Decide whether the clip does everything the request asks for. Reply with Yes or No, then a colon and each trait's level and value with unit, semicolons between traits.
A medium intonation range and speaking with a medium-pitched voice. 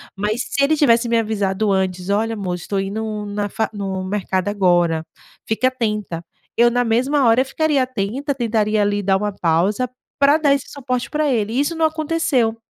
No: average, 4.5 semitones; high, 220 Hz